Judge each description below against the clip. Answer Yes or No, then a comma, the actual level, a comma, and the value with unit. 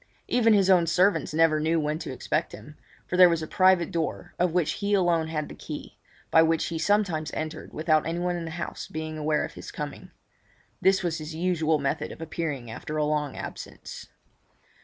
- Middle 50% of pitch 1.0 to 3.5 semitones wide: Yes, narrow, 2.4 semitones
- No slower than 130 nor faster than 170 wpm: No, average, 200 wpm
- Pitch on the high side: No, medium, 165 Hz